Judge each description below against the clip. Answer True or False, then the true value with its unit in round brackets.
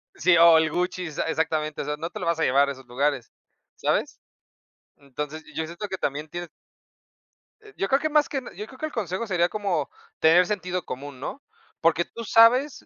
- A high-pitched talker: False (170 Hz)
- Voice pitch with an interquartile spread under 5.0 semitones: False (5.5 semitones)